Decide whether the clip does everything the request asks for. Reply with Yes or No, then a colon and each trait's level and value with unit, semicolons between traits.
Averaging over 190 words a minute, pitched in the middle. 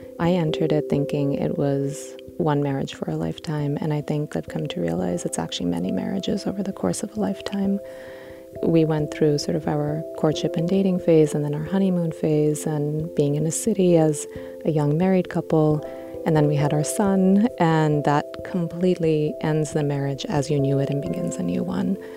Yes: average, 200 wpm; medium, 150 Hz